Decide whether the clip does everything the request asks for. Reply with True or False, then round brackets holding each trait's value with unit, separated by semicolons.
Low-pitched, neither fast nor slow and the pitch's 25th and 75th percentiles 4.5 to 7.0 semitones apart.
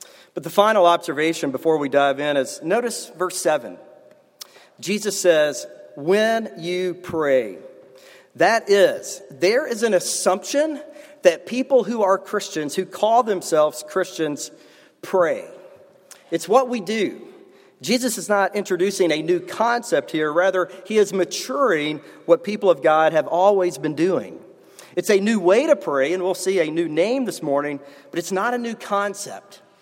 False (190 Hz; 155 wpm; 5.1 semitones)